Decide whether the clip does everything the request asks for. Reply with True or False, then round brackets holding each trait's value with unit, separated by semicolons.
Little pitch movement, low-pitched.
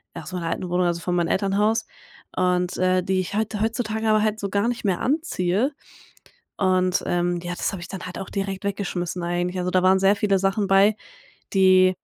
False (2.3 semitones; 190 Hz)